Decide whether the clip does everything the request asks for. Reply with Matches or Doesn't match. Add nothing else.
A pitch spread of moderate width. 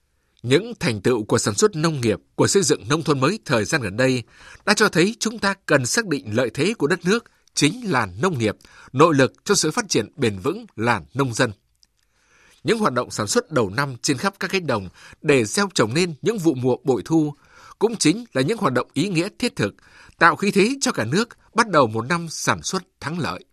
Doesn't match